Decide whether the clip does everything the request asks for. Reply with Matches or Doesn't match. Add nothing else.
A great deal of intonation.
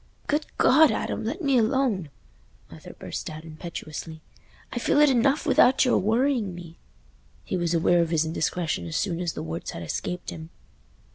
Matches